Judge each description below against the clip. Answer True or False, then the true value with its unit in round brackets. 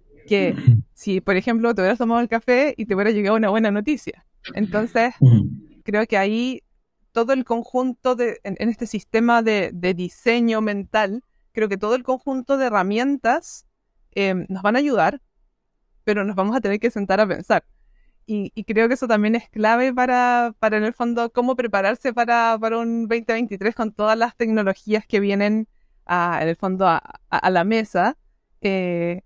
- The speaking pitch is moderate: False (220 Hz)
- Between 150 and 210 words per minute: True (180 wpm)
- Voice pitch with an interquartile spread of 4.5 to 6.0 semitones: False (2.9 semitones)